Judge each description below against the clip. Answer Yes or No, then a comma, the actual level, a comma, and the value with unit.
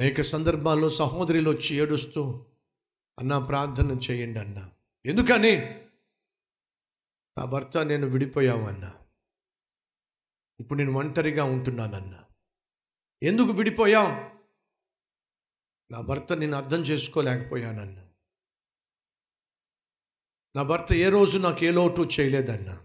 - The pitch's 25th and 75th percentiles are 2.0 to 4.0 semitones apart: No, average, 5.0 semitones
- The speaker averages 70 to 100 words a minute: Yes, average, 85 wpm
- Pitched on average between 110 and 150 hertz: Yes, medium, 140 Hz